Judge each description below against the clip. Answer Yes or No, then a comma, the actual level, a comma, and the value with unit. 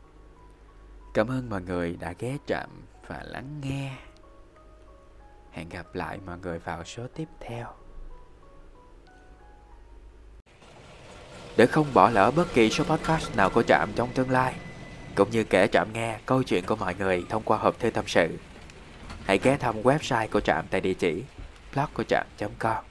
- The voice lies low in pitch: Yes, low, 110 Hz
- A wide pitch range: Yes, wide, 6.1 semitones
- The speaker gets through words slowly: Yes, slow, 160 wpm